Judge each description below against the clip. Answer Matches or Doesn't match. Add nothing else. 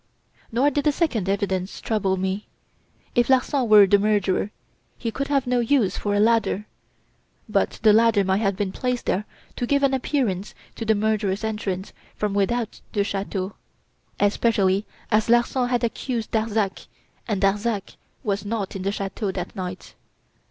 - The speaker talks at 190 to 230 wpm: Doesn't match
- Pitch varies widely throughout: Doesn't match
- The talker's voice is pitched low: Doesn't match